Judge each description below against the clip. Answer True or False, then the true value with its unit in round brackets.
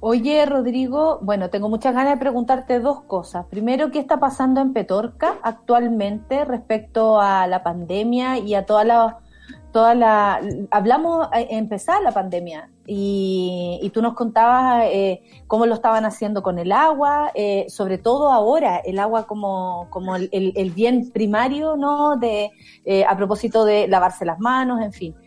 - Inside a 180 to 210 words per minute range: False (160 wpm)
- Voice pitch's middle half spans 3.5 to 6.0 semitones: True (4.4 semitones)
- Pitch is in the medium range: False (225 Hz)